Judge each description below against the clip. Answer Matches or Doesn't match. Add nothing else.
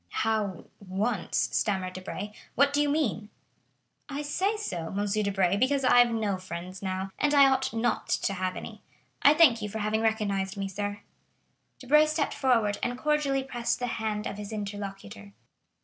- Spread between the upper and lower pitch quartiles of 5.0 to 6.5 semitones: Matches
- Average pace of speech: Matches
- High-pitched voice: Matches